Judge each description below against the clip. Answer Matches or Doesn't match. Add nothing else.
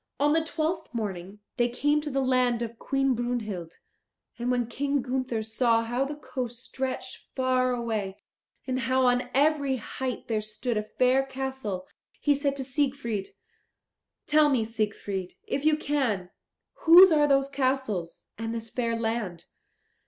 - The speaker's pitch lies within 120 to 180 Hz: Doesn't match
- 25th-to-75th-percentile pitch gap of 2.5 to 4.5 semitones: Matches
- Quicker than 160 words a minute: Doesn't match